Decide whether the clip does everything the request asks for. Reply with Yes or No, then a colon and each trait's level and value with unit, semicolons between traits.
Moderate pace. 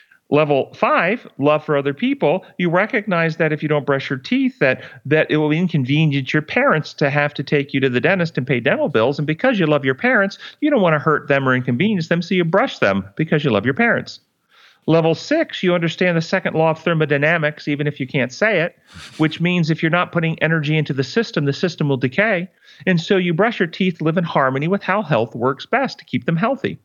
No: fast, 235 wpm